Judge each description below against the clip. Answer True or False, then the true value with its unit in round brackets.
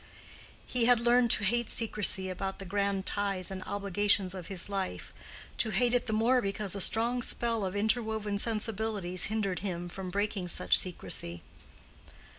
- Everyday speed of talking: True (155 wpm)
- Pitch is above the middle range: True (205 Hz)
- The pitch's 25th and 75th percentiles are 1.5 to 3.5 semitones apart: True (2.8 semitones)